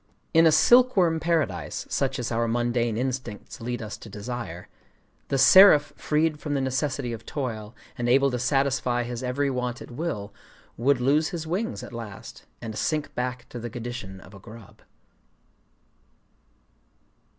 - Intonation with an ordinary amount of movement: Yes, average, 3.8 semitones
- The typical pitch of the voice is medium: No, low, 125 Hz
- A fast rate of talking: No, average, 155 wpm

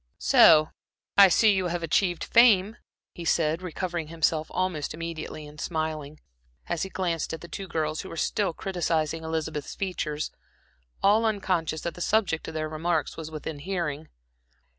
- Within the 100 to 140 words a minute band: No, average, 160 wpm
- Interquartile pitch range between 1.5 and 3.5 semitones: Yes, average, 2.9 semitones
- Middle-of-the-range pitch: Yes, medium, 165 Hz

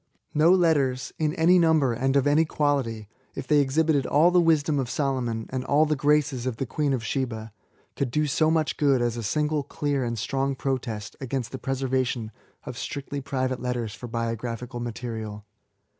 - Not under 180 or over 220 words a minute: Yes, average, 185 wpm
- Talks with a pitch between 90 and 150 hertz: Yes, low, 135 Hz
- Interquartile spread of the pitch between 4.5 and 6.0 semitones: No, average, 3.7 semitones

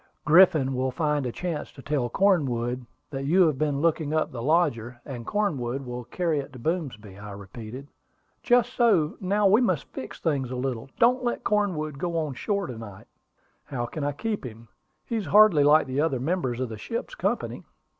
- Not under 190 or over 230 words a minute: Yes, average, 195 wpm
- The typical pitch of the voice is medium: Yes, medium, 145 Hz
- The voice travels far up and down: Yes, wide, 6.2 semitones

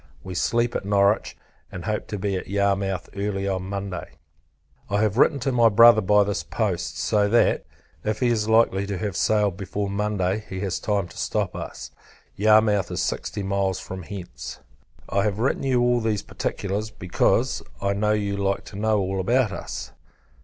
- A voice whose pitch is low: Yes, low, 100 Hz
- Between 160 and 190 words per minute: Yes, average, 180 wpm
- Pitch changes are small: Yes, narrow, 1.9 semitones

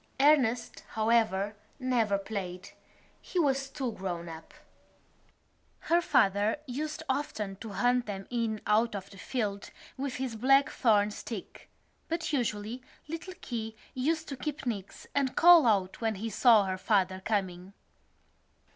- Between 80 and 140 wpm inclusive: Yes, slow, 135 wpm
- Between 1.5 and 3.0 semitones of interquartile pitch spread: No, average, 5.0 semitones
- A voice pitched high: Yes, high, 225 Hz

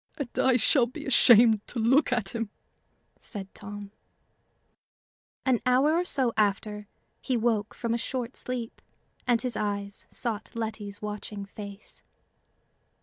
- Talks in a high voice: Yes, high, 225 Hz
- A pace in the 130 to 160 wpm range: Yes, slow, 135 wpm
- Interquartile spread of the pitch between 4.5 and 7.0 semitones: No, average, 3.2 semitones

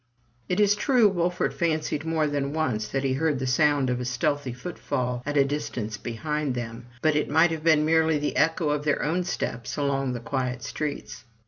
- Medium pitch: Yes, medium, 145 Hz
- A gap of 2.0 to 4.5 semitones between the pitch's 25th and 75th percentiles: Yes, average, 4.0 semitones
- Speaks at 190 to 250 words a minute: Yes, average, 200 wpm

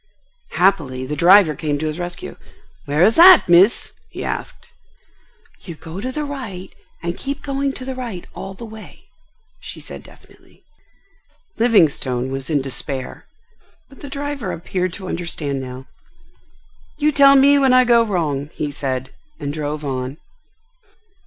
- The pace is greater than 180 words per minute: No, average, 150 wpm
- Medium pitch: Yes, medium, 180 Hz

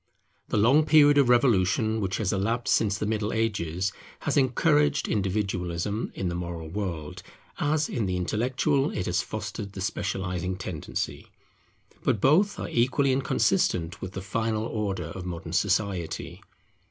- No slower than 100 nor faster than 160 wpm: Yes, average, 145 wpm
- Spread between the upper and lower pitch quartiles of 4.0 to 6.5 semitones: Yes, average, 4.5 semitones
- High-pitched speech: No, low, 105 Hz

